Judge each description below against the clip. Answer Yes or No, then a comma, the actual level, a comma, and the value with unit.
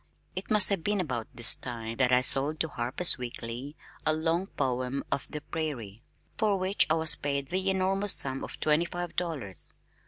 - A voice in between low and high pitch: Yes, medium, 150 Hz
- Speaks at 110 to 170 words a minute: No, average, 185 wpm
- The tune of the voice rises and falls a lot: Yes, wide, 5.9 semitones